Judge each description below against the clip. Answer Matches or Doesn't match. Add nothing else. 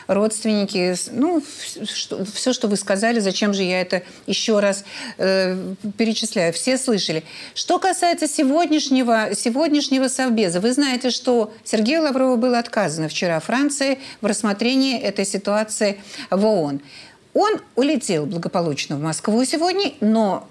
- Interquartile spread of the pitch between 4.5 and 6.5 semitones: Matches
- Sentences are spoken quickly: Doesn't match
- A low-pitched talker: Doesn't match